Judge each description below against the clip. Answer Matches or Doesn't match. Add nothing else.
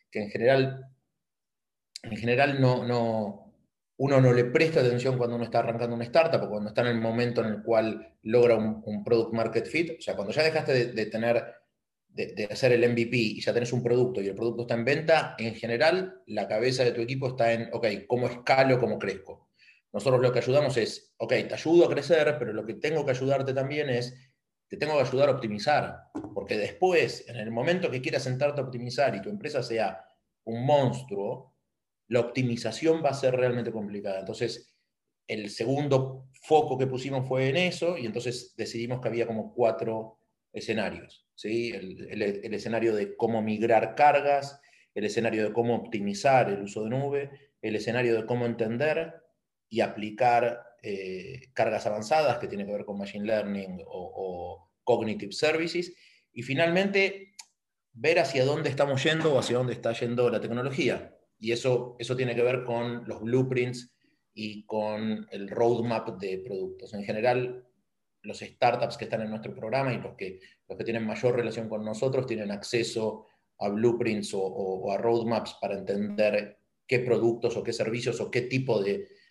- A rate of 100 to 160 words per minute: Doesn't match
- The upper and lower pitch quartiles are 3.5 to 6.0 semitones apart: Doesn't match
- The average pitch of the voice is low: Matches